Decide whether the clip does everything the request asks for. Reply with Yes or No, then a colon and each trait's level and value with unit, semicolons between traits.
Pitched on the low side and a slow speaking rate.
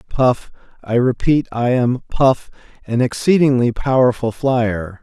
Yes: low, 125 Hz; slow, 85 wpm